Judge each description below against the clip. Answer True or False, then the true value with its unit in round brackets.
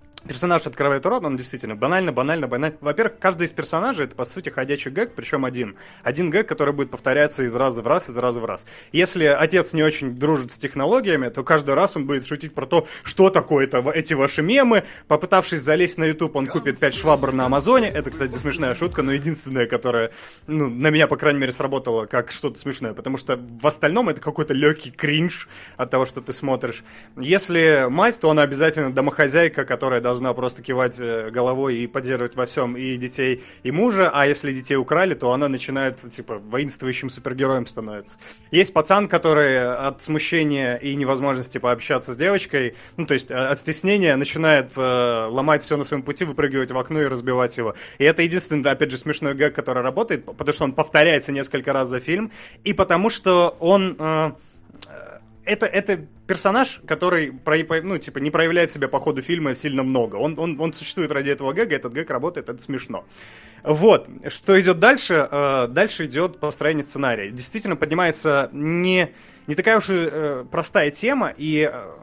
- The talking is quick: True (180 wpm)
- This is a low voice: False (145 Hz)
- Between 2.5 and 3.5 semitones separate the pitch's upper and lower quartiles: False (4.0 semitones)